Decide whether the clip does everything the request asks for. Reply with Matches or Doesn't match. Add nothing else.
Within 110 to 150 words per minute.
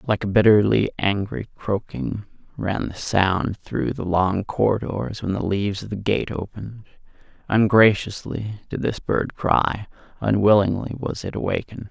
Matches